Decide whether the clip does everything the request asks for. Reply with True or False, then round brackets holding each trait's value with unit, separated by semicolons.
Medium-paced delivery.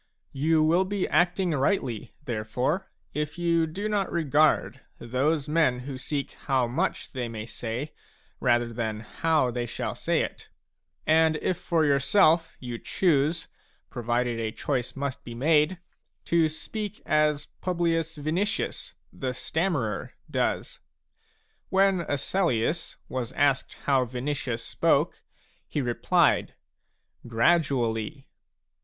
False (120 wpm)